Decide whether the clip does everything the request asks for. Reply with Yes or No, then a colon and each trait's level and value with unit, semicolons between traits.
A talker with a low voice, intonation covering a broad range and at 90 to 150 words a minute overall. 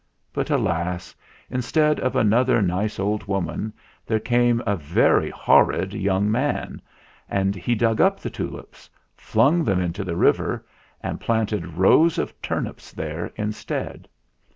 No: low, 105 Hz; average, 4.1 semitones; slow, 135 wpm